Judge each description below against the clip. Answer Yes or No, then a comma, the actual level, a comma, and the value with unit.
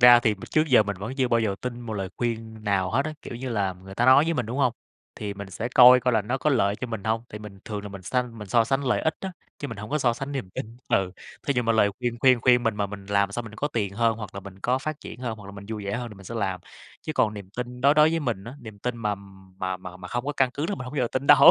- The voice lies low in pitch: Yes, low, 115 Hz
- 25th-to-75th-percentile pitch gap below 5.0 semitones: Yes, average, 3.9 semitones